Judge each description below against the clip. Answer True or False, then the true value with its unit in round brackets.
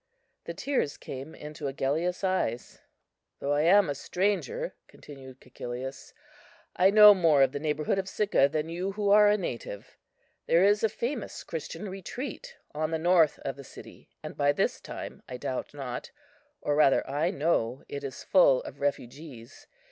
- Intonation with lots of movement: True (5.9 semitones)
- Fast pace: False (165 wpm)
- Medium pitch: True (155 Hz)